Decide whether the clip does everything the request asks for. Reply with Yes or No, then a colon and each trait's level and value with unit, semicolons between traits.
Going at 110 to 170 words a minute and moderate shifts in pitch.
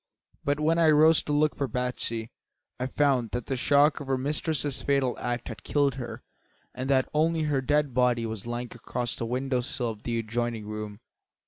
No: average, 195 wpm; average, 3.4 semitones